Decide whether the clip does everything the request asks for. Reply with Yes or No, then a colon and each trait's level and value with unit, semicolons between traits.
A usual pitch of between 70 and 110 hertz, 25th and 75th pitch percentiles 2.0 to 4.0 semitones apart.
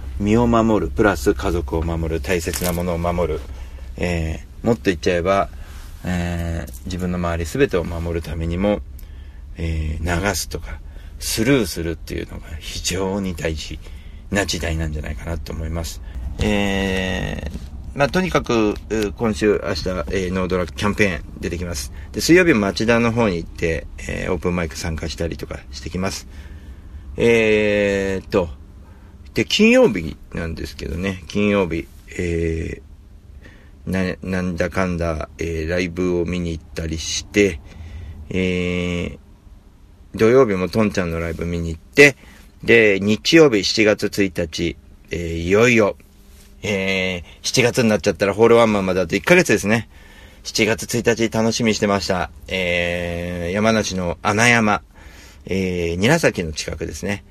Yes: very low, 85 Hz; average, 3.7 semitones